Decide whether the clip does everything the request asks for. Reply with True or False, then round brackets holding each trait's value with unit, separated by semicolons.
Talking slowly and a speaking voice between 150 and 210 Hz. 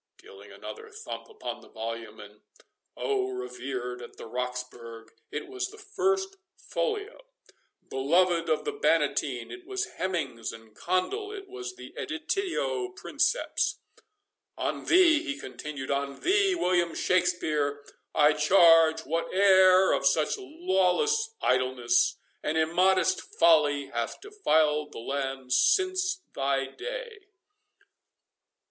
True (110 wpm; 185 Hz)